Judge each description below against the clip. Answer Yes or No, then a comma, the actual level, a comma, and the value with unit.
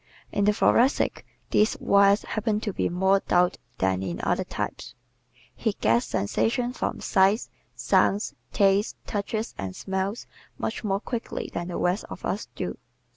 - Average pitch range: Yes, average, 3.3 semitones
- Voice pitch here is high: Yes, high, 200 Hz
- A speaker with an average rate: Yes, average, 155 wpm